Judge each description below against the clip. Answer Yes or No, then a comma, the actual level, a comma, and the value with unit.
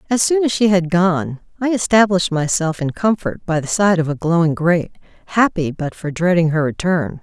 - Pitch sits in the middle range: Yes, medium, 180 Hz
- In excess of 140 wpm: Yes, average, 200 wpm